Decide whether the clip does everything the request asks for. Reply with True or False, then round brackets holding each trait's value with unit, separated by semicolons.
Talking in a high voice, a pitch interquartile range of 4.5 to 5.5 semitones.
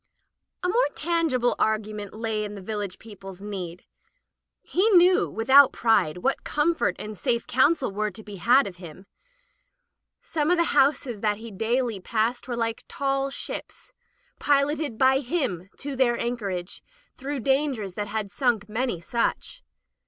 True (235 Hz; 4.8 semitones)